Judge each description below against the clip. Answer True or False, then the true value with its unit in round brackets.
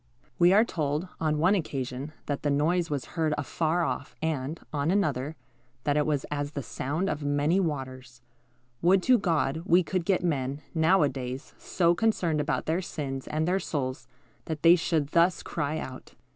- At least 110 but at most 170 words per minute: False (180 wpm)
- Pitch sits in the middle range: True (155 Hz)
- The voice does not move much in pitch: False (3.4 semitones)